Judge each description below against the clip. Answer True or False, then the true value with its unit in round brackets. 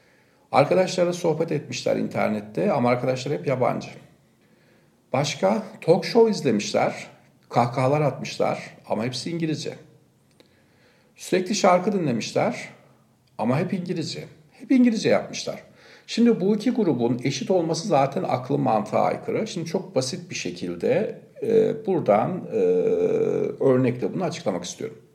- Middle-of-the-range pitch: True (180 Hz)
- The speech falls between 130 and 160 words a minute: False (110 wpm)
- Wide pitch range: True (7.9 semitones)